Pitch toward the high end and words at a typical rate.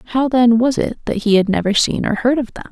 No: high, 235 Hz; fast, 290 wpm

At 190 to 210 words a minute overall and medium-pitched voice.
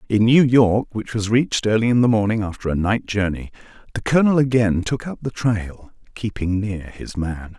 No: average, 200 wpm; low, 110 Hz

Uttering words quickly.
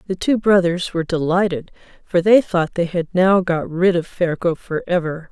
No: average, 190 wpm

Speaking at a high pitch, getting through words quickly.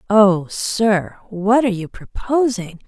No: high, 205 Hz; slow, 125 wpm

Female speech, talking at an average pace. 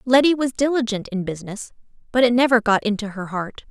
Yes: female; average, 195 wpm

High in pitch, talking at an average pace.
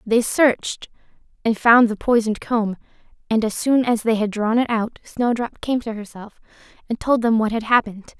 Yes: high, 225 Hz; average, 190 wpm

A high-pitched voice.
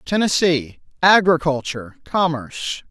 No: medium, 155 Hz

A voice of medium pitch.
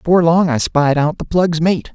Yes: medium, 165 Hz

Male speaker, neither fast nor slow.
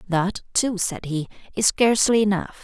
No: female; average, 160 wpm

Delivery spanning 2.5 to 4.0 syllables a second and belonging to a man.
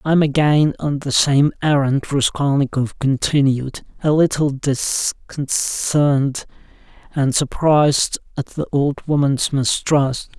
Yes: 3.8 syllables/s; male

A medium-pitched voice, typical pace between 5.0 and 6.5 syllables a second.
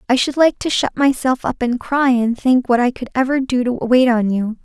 No: very high, 250 Hz; 5.1 syllables/s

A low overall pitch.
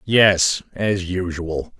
Yes: very low, 95 Hz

